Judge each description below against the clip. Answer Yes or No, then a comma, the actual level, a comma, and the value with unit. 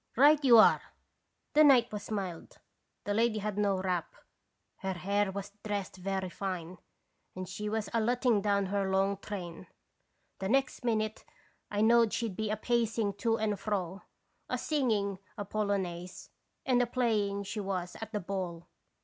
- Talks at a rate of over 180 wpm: No, average, 165 wpm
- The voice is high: Yes, high, 205 Hz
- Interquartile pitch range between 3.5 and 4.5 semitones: No, average, 2.7 semitones